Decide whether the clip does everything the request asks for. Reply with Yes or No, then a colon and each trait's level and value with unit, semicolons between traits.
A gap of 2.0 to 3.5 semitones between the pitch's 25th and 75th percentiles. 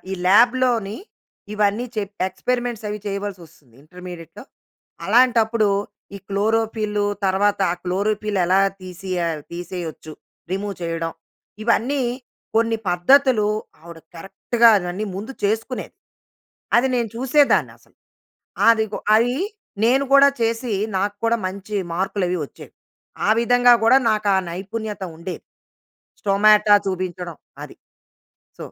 No: average, 3.9 semitones